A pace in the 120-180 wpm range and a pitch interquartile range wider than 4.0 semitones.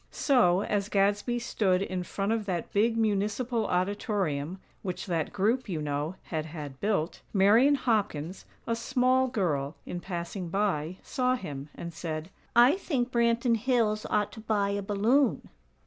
Yes: average, 150 wpm; average, 4.9 semitones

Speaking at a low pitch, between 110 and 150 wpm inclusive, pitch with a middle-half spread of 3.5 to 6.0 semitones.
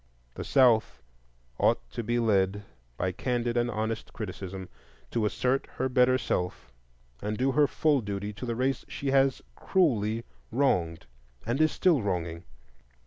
Yes: low, 115 Hz; average, 145 wpm; average, 4.5 semitones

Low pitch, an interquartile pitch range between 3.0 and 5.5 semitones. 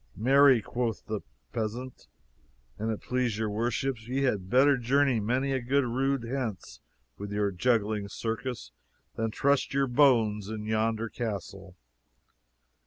Yes: low, 115 Hz; average, 3.5 semitones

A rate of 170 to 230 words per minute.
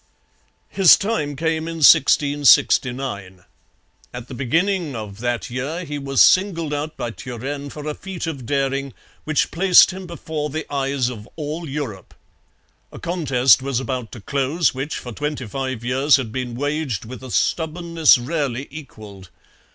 No: average, 150 wpm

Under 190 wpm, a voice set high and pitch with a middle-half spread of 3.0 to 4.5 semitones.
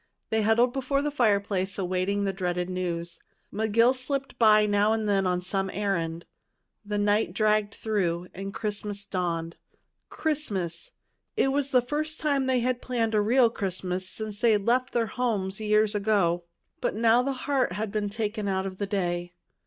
Yes: average, 170 wpm; high, 210 Hz; average, 3.8 semitones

